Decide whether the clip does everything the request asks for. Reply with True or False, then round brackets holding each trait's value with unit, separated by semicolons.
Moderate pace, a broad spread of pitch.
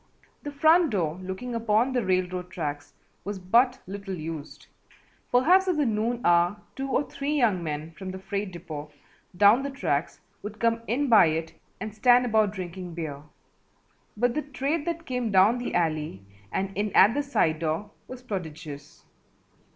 True (165 wpm; 6.3 semitones)